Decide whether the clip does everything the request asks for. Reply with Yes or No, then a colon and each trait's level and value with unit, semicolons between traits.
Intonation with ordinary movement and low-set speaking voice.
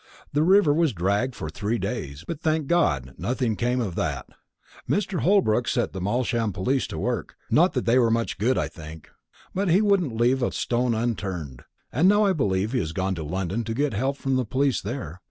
No: wide, 6.7 semitones; low, 120 Hz